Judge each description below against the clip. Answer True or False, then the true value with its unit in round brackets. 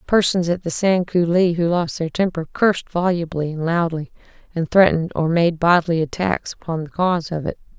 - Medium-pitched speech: True (170 Hz)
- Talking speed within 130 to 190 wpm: True (185 wpm)